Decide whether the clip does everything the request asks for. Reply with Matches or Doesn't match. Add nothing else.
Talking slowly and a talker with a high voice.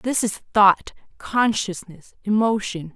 Matches